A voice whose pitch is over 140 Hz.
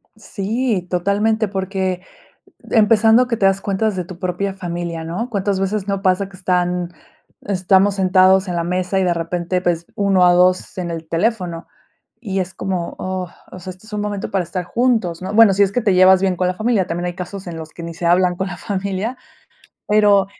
Yes: high, 190 Hz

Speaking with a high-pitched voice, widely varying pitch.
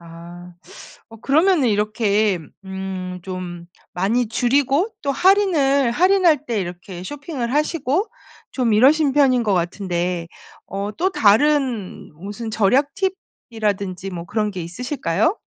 Yes: high, 225 Hz; wide, 6.9 semitones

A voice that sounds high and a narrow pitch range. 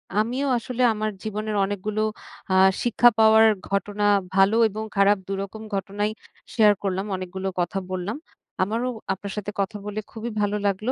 Yes: high, 210 Hz; narrow, 1.8 semitones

